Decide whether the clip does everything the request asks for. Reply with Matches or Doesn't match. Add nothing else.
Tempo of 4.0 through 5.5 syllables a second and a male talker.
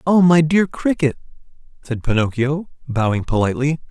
Matches